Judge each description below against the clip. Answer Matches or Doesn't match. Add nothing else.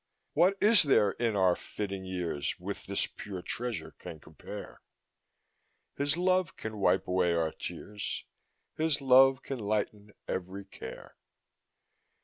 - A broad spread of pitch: Matches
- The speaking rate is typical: Doesn't match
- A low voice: Matches